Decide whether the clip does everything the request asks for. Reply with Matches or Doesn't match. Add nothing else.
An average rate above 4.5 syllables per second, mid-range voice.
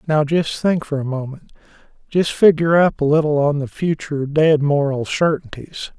Matches